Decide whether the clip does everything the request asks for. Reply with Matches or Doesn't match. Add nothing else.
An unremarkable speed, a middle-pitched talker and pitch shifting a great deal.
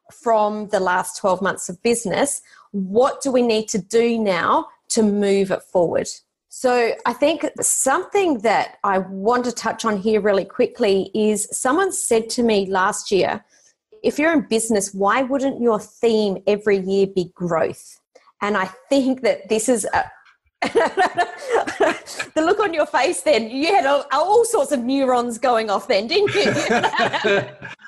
Doesn't match